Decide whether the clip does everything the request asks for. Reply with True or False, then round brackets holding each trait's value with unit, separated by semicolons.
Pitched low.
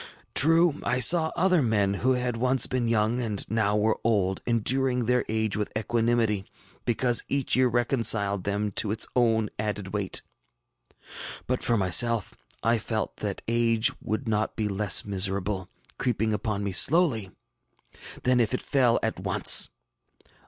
True (115 Hz)